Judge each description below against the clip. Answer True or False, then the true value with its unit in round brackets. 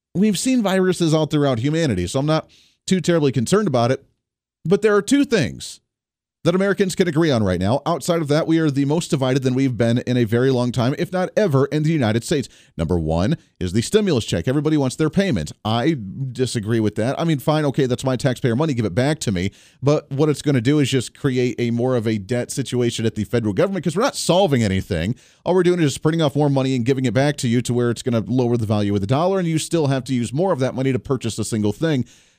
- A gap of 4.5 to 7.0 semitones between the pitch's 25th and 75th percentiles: True (5.1 semitones)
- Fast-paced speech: True (260 wpm)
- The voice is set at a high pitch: False (135 Hz)